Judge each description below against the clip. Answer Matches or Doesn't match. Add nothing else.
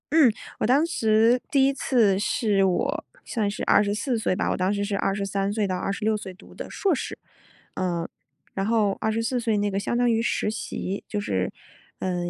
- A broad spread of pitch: Doesn't match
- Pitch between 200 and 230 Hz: Matches